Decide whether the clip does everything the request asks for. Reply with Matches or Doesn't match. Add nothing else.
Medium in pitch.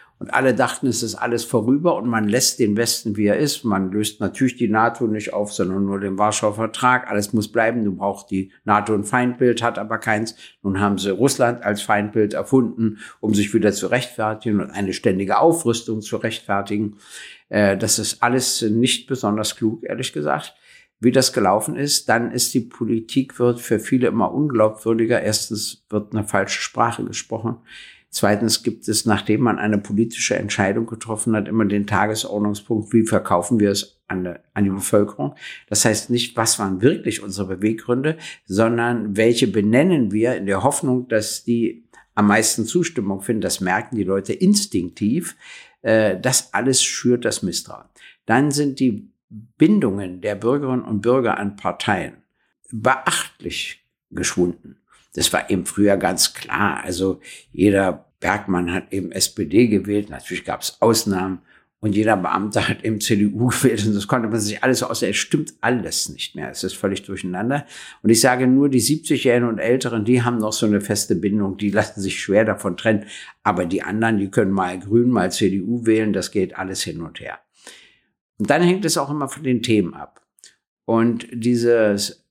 Doesn't match